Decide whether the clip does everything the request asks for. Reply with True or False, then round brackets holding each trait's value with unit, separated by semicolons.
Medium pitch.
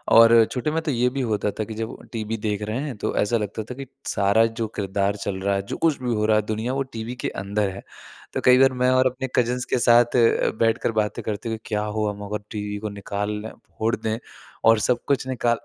False (110 Hz)